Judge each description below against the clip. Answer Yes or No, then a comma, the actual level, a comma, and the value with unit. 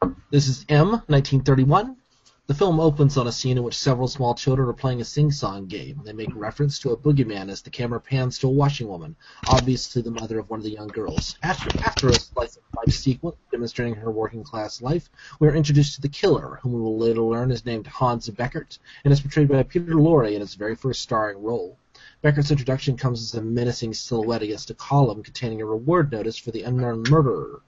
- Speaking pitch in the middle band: No, low, 130 Hz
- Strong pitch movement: No, average, 4.0 semitones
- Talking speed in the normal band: No, fast, 215 wpm